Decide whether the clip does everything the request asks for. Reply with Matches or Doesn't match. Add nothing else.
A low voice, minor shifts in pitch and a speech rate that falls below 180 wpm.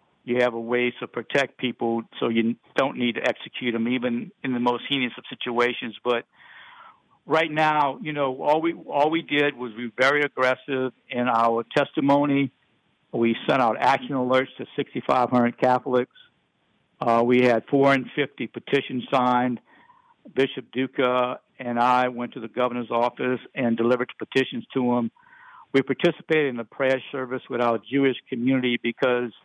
Matches